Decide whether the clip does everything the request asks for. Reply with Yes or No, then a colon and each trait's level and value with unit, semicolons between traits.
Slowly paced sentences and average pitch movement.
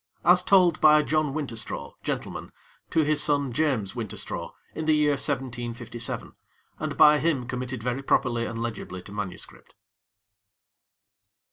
Yes: slow, 130 wpm; average, 4.5 semitones